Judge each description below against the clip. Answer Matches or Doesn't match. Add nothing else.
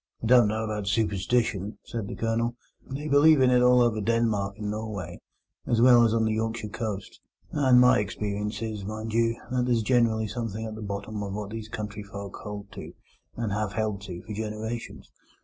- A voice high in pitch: Doesn't match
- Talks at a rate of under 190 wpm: Doesn't match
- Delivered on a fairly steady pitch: Matches